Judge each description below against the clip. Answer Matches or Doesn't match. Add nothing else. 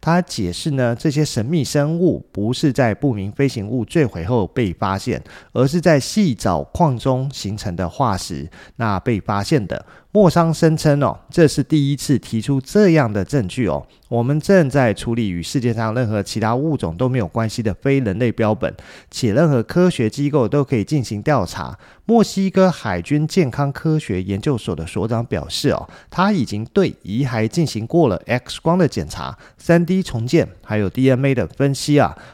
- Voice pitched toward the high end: Doesn't match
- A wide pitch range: Matches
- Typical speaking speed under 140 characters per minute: Doesn't match